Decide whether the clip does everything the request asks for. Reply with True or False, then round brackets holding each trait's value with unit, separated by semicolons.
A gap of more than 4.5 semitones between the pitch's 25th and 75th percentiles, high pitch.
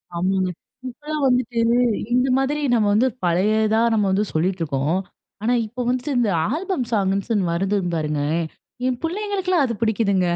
True (5.2 semitones; 220 Hz)